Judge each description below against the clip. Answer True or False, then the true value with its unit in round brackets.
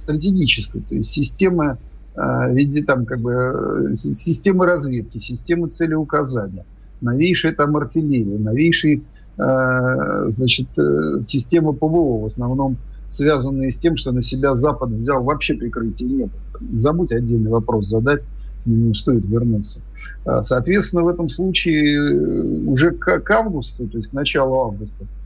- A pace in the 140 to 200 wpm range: False (125 wpm)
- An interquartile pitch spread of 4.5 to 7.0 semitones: True (5.1 semitones)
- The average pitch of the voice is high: False (130 Hz)